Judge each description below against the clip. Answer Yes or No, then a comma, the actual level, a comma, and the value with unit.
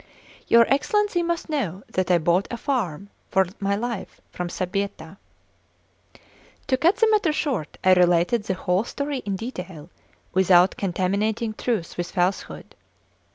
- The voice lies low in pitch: No, high, 200 Hz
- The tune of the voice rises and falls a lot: Yes, wide, 5.8 semitones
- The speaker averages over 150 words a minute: No, average, 145 wpm